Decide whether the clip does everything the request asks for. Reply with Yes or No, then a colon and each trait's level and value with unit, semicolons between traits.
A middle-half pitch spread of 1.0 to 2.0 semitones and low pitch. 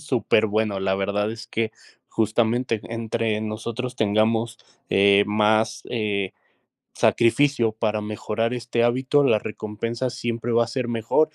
Yes: narrow, 1.7 semitones; low, 110 Hz